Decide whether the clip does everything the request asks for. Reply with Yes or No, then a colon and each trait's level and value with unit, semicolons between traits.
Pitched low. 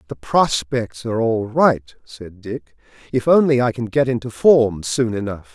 Yes: low, 115 Hz